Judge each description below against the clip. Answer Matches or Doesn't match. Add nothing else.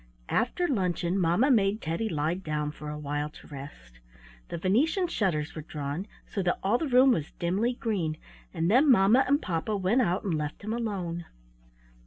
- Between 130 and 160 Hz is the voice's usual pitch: Doesn't match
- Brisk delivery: Doesn't match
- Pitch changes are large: Matches